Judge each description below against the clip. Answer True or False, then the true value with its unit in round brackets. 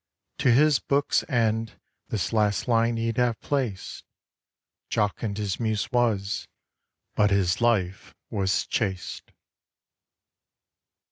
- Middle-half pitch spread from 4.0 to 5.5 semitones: False (2.9 semitones)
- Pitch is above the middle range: False (110 Hz)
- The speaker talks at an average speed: False (105 wpm)